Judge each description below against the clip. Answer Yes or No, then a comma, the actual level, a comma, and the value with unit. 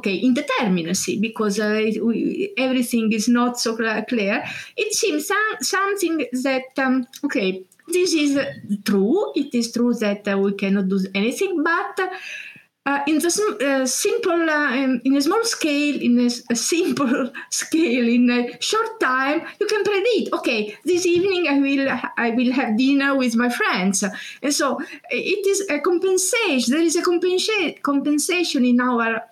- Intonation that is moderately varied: No, wide, 6.5 semitones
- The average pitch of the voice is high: Yes, very high, 275 Hz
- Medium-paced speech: Yes, average, 160 wpm